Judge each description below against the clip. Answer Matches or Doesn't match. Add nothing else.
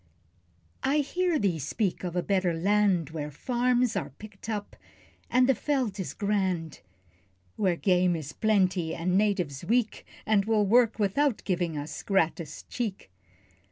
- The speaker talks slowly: Doesn't match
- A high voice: Matches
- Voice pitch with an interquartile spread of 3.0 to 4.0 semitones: Doesn't match